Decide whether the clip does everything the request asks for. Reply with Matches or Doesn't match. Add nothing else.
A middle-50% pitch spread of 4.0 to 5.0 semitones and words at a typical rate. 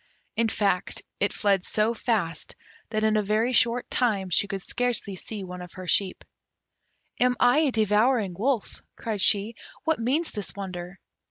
Doesn't match